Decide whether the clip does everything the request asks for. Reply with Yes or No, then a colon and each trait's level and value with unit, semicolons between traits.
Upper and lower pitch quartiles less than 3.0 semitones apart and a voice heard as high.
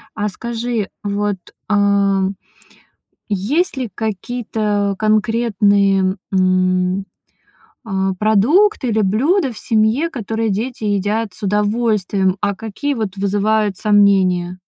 Yes: narrow, 2.5 semitones; high, 205 Hz